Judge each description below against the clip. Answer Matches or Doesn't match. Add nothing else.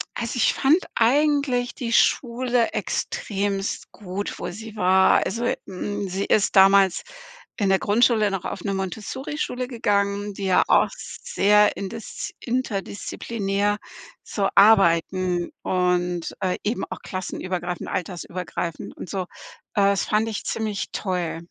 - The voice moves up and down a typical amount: Matches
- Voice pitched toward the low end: Doesn't match